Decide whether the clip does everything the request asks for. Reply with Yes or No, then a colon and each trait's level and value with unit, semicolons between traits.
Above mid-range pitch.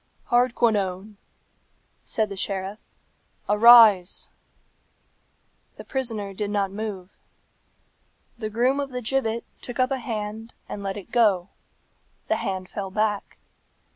Yes: high, 215 Hz